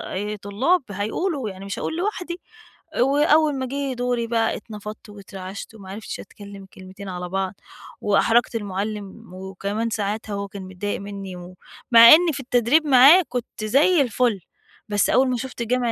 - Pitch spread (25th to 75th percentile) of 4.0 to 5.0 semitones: Yes, average, 4.5 semitones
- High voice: Yes, high, 220 Hz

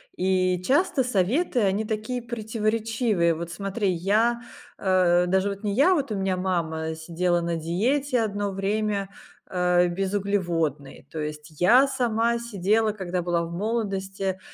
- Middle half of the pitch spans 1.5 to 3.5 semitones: No, average, 4.0 semitones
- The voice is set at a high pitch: Yes, high, 195 Hz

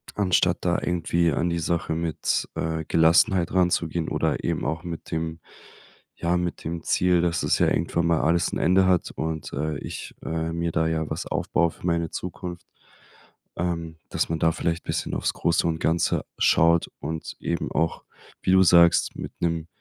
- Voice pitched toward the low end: Yes, very low, 85 Hz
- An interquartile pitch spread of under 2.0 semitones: Yes, narrow, 1.2 semitones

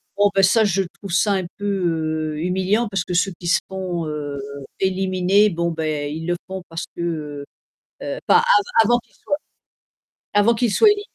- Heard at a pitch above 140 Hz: Yes, high, 190 Hz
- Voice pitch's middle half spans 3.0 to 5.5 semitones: Yes, average, 3.4 semitones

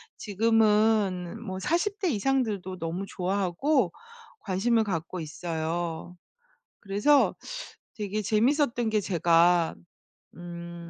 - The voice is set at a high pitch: Yes, high, 195 Hz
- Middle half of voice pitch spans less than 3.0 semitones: No, average, 4.4 semitones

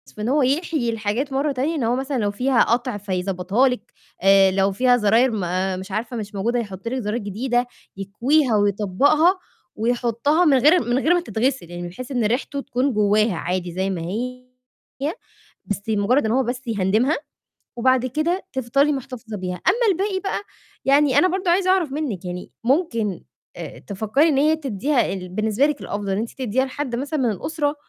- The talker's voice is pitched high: Yes, high, 245 Hz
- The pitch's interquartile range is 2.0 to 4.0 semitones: No, wide, 5.4 semitones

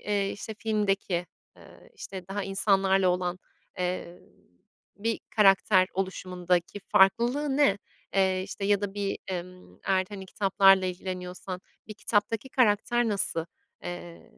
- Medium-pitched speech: No, high, 195 Hz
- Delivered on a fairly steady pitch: Yes, narrow, 2.1 semitones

